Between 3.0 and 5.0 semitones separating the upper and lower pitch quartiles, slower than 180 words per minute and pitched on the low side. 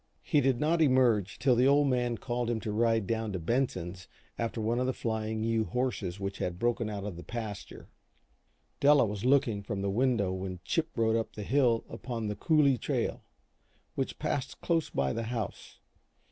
No: average, 3.7 semitones; average, 190 wpm; low, 115 Hz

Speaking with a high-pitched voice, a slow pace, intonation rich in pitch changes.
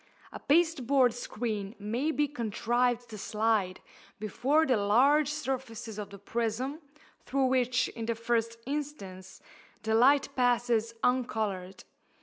No: high, 240 Hz; slow, 125 wpm; average, 3.6 semitones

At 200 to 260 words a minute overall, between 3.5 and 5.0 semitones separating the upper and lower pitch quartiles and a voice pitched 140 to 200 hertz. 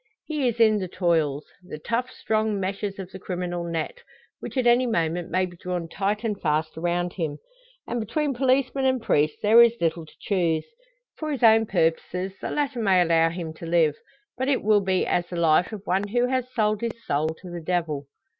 No: fast, 205 wpm; wide, 5.6 semitones; high, 190 Hz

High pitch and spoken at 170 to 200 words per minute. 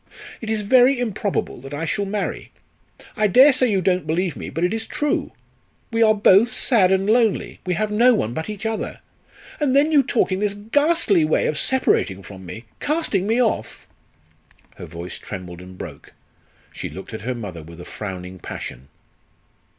Yes: high, 200 Hz; average, 185 wpm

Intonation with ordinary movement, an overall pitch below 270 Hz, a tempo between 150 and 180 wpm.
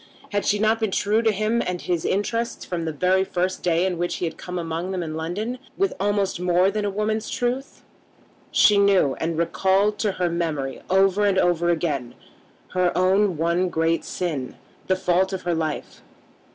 No: average, 3.2 semitones; medium, 185 Hz; average, 190 wpm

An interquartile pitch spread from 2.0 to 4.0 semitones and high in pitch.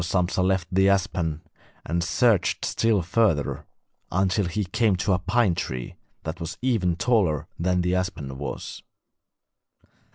No: average, 2.8 semitones; very low, 90 Hz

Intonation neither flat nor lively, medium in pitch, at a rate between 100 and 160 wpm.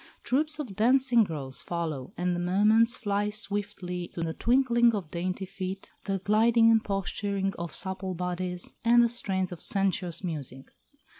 No: average, 4.0 semitones; high, 195 Hz; average, 155 wpm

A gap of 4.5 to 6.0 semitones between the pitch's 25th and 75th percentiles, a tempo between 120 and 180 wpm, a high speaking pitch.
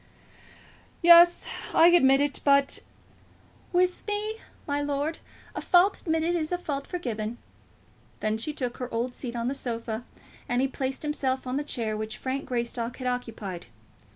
Yes: average, 4.9 semitones; average, 160 wpm; very high, 270 Hz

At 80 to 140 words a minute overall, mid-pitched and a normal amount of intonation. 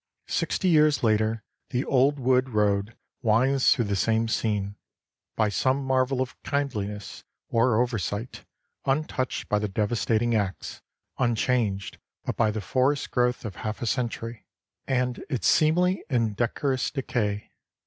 No: slow, 135 wpm; low, 120 Hz; average, 3.5 semitones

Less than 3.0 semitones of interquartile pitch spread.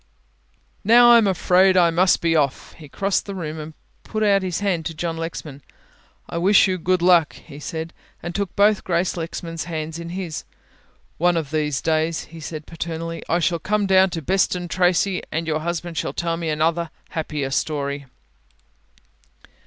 Yes: narrow, 2.6 semitones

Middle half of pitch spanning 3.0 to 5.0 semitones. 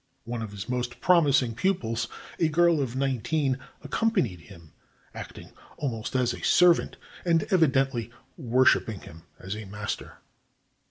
No: wide, 5.4 semitones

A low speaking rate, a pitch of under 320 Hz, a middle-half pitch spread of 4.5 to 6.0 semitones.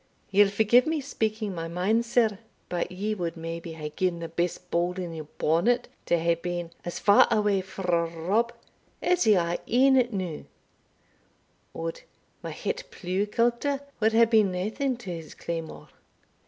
No: average, 160 wpm; high, 190 Hz; average, 4.8 semitones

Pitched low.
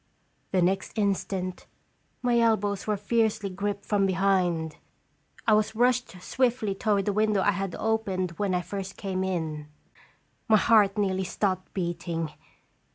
No: high, 195 Hz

